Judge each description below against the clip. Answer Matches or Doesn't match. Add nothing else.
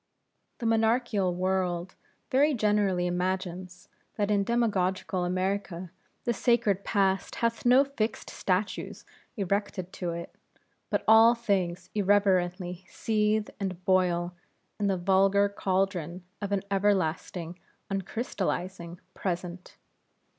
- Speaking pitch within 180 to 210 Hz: Matches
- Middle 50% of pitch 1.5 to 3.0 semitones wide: Matches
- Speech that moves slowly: Matches